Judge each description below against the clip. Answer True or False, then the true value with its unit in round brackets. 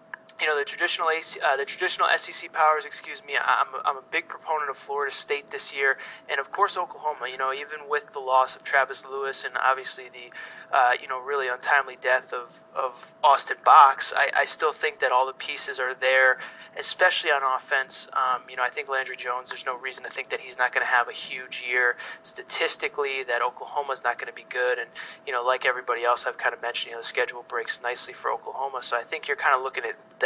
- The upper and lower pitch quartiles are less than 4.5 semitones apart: True (2.6 semitones)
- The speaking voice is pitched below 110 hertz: False (135 Hz)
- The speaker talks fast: True (235 wpm)